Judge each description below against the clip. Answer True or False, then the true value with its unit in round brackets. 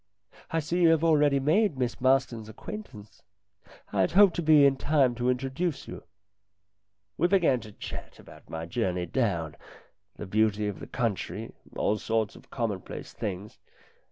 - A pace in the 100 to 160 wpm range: True (155 wpm)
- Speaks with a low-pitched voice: True (125 Hz)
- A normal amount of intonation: False (6.6 semitones)